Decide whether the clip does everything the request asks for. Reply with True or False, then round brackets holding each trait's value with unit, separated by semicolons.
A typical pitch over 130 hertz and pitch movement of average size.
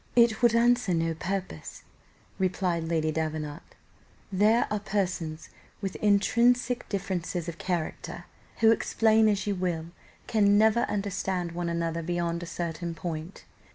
True (185 Hz; 4.0 semitones)